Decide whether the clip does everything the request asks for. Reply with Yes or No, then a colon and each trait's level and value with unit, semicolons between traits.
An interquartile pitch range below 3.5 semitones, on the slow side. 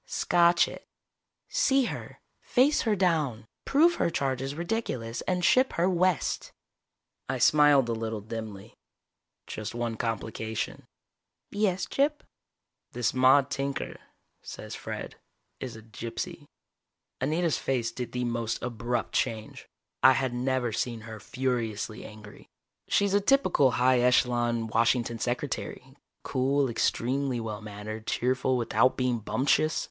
No: average, 4.7 semitones; slow, 125 wpm